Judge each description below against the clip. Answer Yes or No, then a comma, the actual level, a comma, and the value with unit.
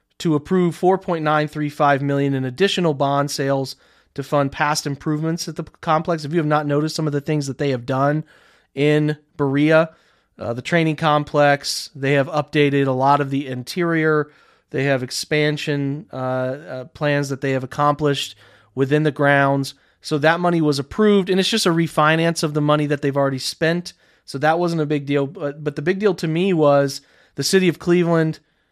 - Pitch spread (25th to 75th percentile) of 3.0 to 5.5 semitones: No, narrow, 2.4 semitones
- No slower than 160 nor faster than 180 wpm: No, average, 190 wpm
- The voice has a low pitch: No, medium, 150 Hz